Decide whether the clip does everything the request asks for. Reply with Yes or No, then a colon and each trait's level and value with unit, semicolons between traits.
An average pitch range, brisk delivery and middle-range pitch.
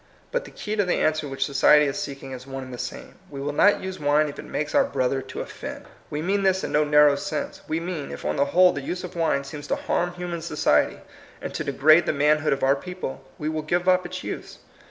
Yes: average, 4.1 semitones; fast, 260 wpm; medium, 150 Hz